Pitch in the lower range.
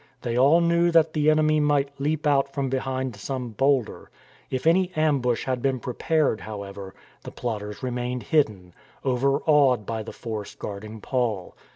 Yes: low, 130 Hz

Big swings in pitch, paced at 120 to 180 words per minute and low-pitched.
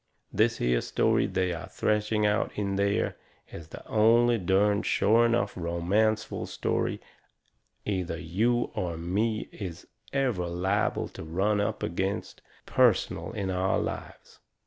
No: average, 3.5 semitones; slow, 135 wpm; low, 100 Hz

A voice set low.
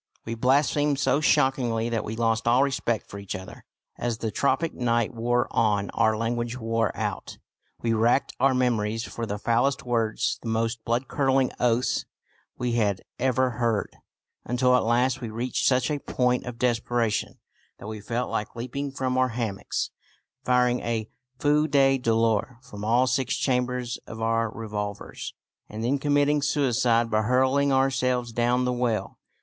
Yes: low, 120 Hz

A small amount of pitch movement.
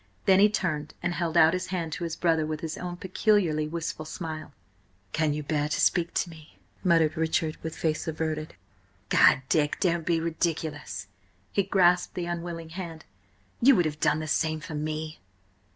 Yes: narrow, 2.1 semitones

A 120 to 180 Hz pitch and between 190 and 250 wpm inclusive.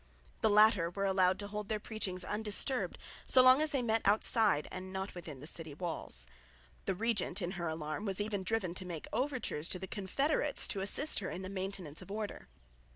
No: high, 195 Hz; average, 200 wpm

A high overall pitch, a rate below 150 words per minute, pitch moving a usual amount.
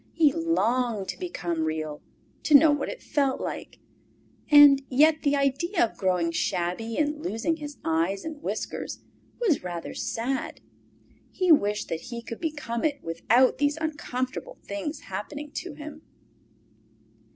No: very high, 275 Hz; average, 140 wpm; wide, 6.9 semitones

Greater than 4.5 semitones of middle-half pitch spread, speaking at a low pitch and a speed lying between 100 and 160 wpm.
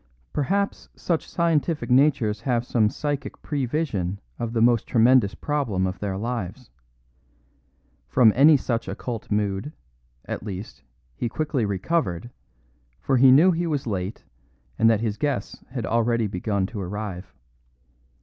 Yes: average, 5.3 semitones; low, 115 Hz; slow, 135 wpm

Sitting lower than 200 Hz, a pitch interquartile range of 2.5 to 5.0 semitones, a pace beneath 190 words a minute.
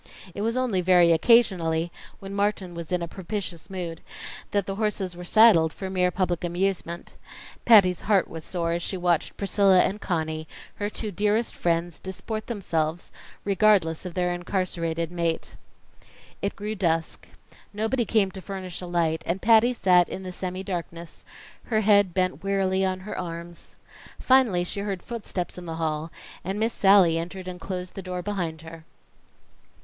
Yes: medium, 185 Hz; average, 2.9 semitones; average, 165 wpm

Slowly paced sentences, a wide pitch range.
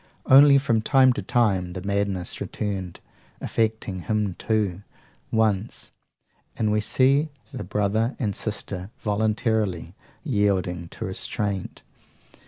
No: slow, 110 wpm; average, 2.9 semitones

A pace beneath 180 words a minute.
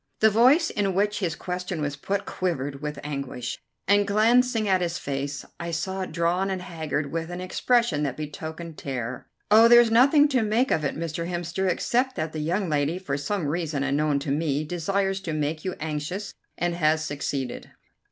No: average, 185 wpm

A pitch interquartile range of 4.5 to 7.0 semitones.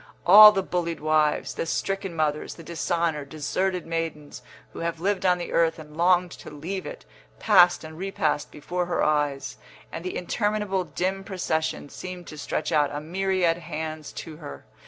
No: average, 3.1 semitones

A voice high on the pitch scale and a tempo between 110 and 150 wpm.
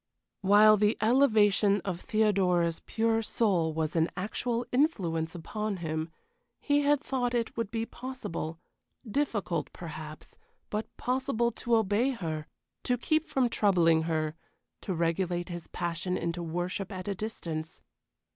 Yes: high, 200 Hz; slow, 135 wpm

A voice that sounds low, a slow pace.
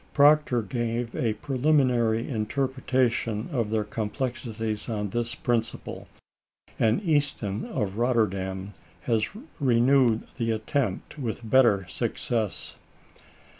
Yes: low, 115 Hz; slow, 95 wpm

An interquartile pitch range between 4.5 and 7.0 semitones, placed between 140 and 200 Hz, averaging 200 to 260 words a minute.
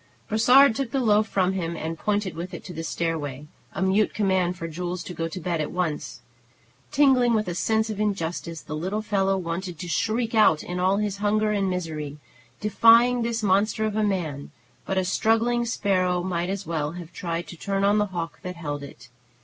No: average, 4.1 semitones; high, 190 Hz; fast, 205 wpm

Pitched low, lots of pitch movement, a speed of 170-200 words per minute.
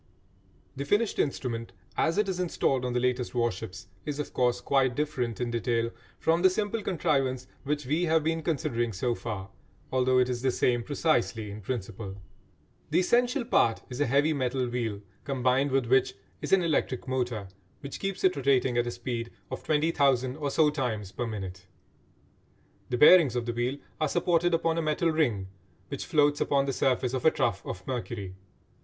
No: low, 130 Hz; average, 4.4 semitones; average, 180 wpm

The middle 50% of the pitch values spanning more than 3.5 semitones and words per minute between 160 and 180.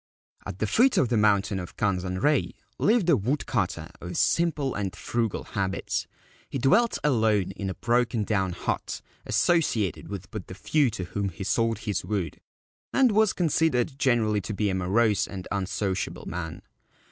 Yes: wide, 5.6 semitones; average, 165 wpm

